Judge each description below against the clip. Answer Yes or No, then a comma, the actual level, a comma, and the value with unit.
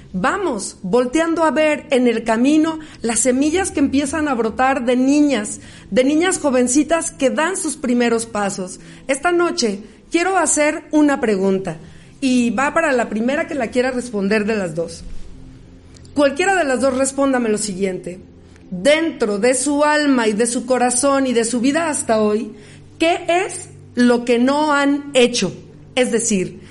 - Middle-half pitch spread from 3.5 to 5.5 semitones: Yes, average, 4.9 semitones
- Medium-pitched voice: No, very high, 255 Hz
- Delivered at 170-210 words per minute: No, average, 160 wpm